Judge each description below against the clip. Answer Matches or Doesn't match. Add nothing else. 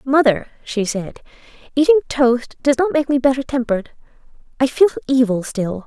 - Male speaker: Doesn't match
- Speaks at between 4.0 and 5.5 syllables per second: Matches